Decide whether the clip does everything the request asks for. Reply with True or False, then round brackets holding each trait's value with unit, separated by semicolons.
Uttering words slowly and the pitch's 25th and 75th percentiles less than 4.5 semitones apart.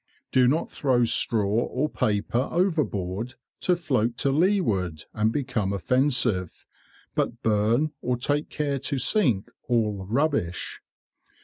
False (120 wpm; 5.3 semitones)